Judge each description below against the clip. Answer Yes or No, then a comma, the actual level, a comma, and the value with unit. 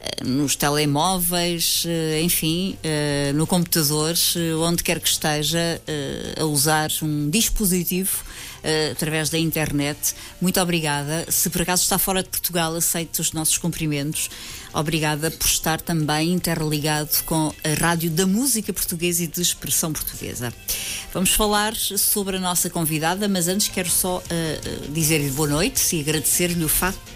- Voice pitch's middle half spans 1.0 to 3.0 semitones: Yes, average, 2.7 semitones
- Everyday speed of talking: Yes, average, 135 wpm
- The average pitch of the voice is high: No, medium, 165 Hz